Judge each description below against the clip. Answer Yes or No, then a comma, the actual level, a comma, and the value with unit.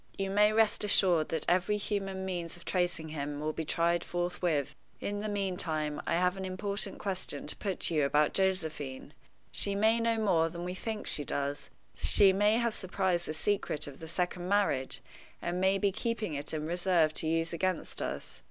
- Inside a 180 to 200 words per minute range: Yes, average, 190 wpm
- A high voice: No, medium, 180 Hz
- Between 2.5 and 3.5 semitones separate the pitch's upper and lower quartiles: No, average, 3.9 semitones